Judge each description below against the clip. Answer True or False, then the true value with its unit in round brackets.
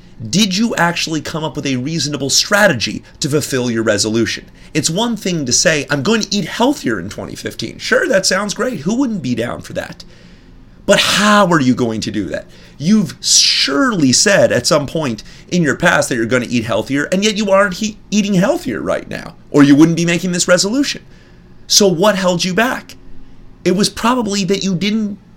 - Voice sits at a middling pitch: True (180 Hz)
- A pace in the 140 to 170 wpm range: False (200 wpm)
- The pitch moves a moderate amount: False (6.5 semitones)